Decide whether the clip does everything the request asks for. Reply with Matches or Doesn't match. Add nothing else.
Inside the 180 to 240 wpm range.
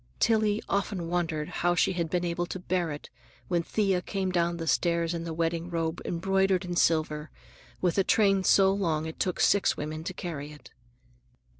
Matches